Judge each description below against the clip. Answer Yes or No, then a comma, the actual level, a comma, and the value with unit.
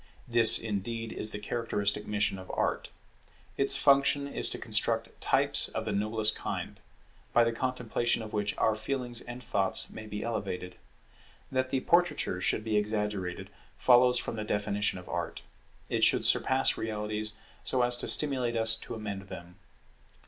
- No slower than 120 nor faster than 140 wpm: No, average, 160 wpm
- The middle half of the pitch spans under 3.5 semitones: Yes, average, 2.8 semitones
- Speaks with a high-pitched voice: No, low, 110 Hz